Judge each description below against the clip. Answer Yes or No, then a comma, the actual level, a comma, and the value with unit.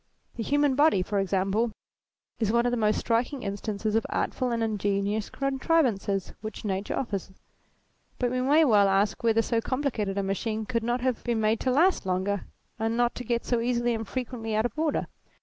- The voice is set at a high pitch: Yes, high, 225 Hz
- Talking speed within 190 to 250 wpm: Yes, average, 195 wpm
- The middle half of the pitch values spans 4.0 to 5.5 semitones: No, average, 3.4 semitones